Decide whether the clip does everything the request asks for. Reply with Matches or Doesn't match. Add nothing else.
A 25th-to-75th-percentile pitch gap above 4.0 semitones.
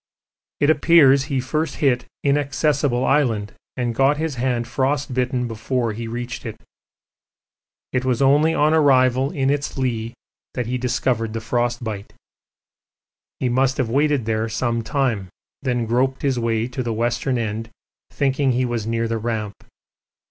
Doesn't match